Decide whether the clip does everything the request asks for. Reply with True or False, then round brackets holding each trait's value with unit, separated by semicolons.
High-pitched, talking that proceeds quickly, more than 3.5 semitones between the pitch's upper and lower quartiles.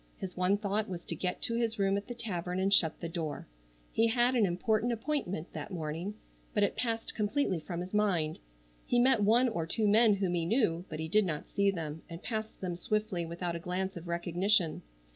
True (195 Hz; 215 wpm; 4.2 semitones)